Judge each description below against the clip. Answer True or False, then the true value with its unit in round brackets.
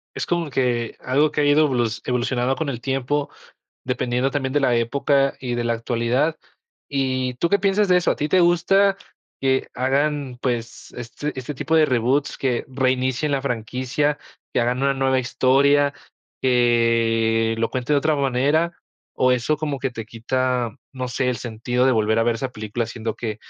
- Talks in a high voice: False (130 Hz)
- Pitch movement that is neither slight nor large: True (3.1 semitones)